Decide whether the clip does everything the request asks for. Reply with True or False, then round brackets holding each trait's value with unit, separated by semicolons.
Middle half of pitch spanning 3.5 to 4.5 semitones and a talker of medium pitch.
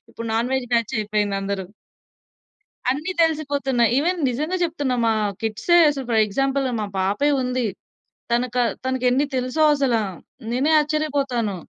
False (4.0 semitones; 255 Hz)